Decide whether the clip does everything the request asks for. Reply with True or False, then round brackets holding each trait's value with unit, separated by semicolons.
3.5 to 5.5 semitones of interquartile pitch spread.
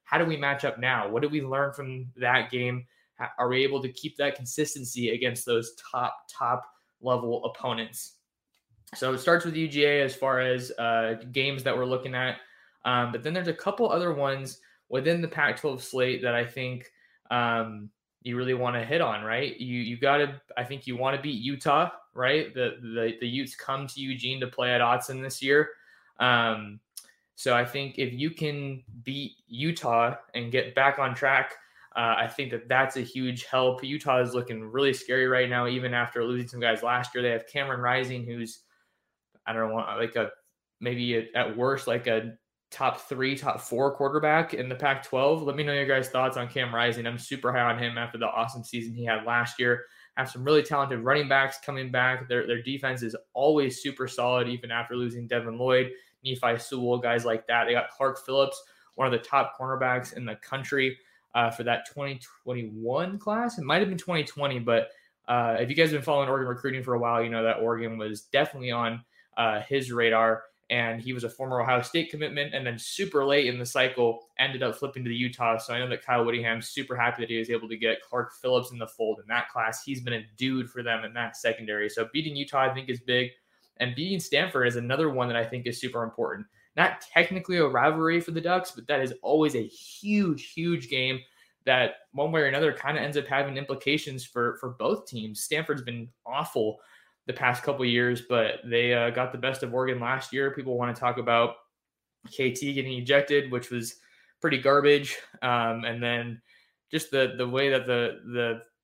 False (2.6 semitones)